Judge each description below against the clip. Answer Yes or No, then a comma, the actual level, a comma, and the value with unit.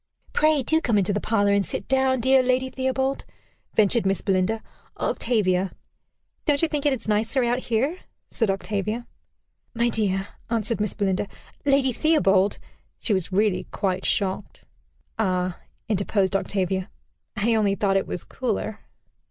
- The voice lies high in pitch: Yes, high, 215 Hz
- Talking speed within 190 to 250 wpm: No, average, 145 wpm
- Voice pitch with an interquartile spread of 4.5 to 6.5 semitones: Yes, average, 4.8 semitones